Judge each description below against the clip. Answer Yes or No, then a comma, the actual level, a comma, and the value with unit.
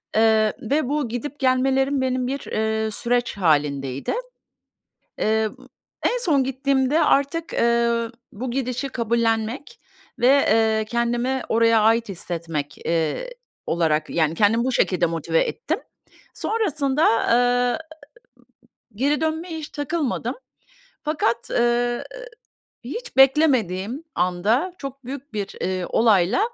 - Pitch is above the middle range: Yes, high, 240 Hz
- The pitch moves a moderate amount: Yes, average, 4.2 semitones